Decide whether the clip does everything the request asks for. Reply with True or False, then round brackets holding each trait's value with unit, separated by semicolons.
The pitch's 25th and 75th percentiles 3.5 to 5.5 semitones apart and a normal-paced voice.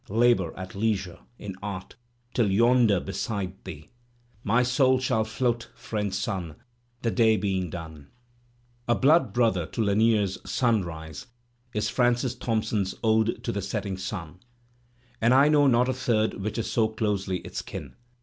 True (3.9 semitones; 155 wpm)